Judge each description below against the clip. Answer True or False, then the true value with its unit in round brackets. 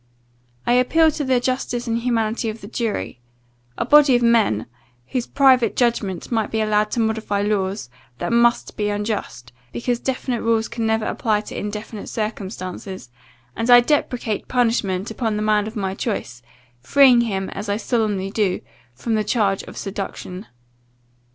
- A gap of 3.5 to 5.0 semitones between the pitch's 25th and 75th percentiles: False (2.8 semitones)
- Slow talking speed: False (160 wpm)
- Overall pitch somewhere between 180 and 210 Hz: False (220 Hz)